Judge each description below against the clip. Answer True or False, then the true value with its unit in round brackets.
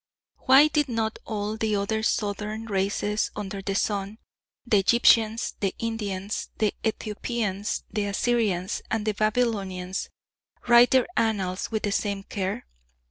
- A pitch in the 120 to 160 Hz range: False (210 Hz)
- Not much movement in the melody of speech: True (2.2 semitones)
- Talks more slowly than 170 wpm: True (135 wpm)